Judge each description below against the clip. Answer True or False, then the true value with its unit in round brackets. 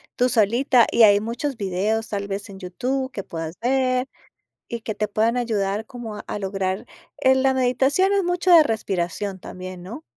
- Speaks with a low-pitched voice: False (225 Hz)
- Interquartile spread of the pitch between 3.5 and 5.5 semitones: True (4.7 semitones)